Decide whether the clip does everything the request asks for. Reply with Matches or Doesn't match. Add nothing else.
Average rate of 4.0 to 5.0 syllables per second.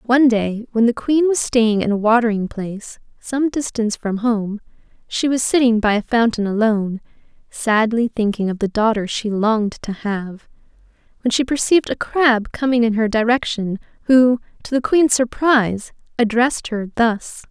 Matches